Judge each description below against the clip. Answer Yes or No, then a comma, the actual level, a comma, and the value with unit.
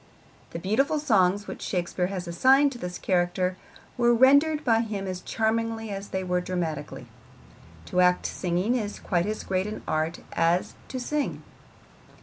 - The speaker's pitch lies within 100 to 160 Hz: No, high, 195 Hz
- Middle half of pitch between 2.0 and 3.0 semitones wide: No, average, 4.7 semitones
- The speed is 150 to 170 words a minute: Yes, average, 155 wpm